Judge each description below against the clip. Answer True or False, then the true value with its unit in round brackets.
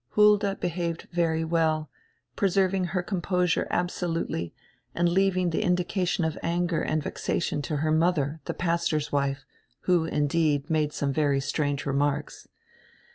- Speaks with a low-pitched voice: False (165 Hz)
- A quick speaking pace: False (135 wpm)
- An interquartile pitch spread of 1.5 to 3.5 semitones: True (3.2 semitones)